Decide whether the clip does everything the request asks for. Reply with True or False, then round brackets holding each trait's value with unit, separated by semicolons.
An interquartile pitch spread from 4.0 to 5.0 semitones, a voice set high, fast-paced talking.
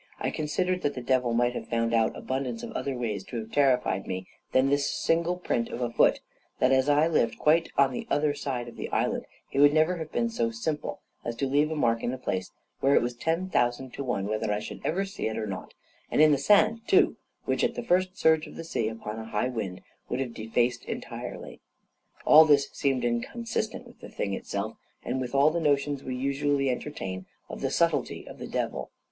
False (4.7 semitones; 130 Hz; 225 wpm)